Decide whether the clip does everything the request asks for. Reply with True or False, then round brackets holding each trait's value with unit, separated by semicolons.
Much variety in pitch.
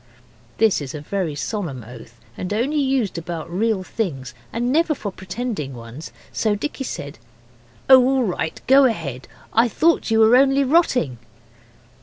True (9.0 semitones)